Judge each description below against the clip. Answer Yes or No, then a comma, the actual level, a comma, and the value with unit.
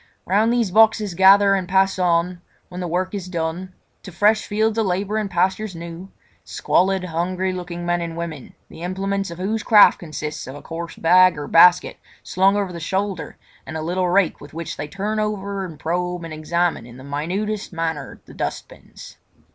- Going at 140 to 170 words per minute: No, average, 185 wpm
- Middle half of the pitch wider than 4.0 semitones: No, average, 2.8 semitones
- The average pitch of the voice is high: No, medium, 180 Hz